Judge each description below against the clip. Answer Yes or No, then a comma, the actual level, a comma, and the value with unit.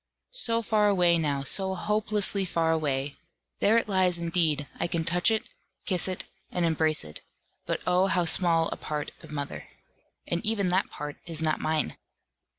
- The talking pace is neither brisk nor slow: Yes, average, 170 wpm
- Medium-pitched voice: Yes, medium, 170 Hz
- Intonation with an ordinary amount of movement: Yes, average, 3.5 semitones